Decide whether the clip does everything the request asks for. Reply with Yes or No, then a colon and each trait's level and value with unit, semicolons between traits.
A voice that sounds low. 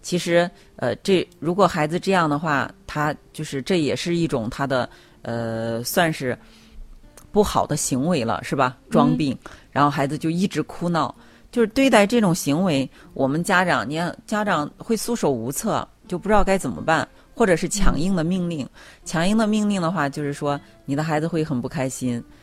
No: medium, 160 Hz